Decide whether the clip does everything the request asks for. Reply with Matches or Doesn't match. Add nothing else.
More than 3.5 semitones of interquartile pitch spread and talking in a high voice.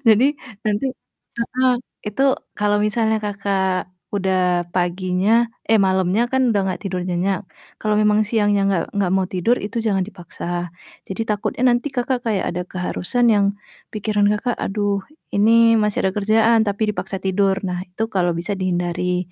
Doesn't match